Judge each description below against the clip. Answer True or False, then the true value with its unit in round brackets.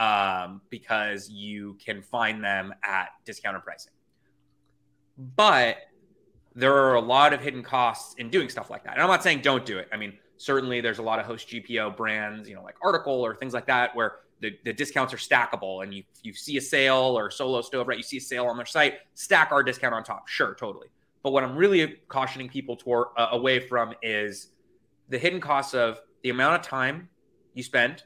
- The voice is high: False (120 Hz)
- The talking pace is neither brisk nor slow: False (210 wpm)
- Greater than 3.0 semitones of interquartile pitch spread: True (4.3 semitones)